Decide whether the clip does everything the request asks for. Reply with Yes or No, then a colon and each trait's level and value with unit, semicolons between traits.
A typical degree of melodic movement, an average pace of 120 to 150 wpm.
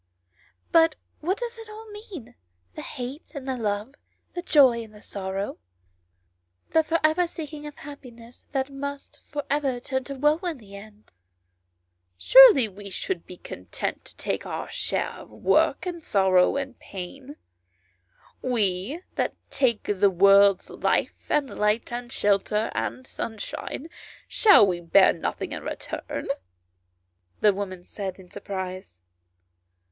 No: wide, 7.1 semitones; average, 145 wpm